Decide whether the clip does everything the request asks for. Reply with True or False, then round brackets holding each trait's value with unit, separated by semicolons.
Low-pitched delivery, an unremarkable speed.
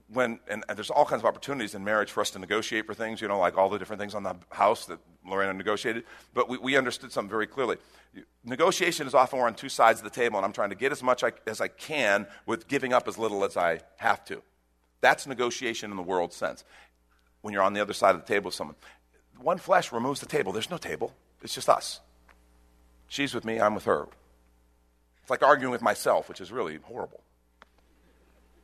False (95 Hz; 230 wpm)